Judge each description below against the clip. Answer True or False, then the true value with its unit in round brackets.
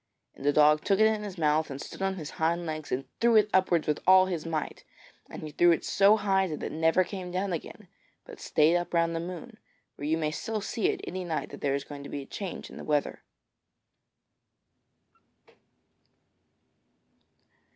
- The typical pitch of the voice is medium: True (170 Hz)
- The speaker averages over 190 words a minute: True (200 wpm)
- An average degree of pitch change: True (3.9 semitones)